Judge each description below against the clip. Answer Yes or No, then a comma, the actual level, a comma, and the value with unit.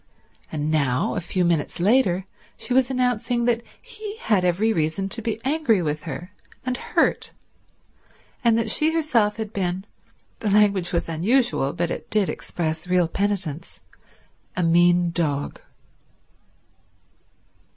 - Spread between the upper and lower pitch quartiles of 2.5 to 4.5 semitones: No, average, 5.3 semitones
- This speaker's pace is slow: Yes, slow, 130 wpm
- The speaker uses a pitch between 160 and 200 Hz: Yes, high, 190 Hz